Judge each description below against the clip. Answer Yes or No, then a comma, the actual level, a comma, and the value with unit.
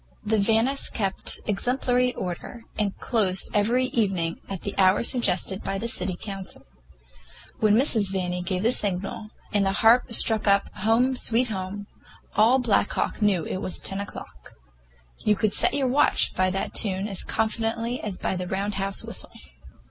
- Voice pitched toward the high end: Yes, high, 205 Hz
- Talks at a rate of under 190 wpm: Yes, average, 165 wpm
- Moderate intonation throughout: Yes, average, 3.0 semitones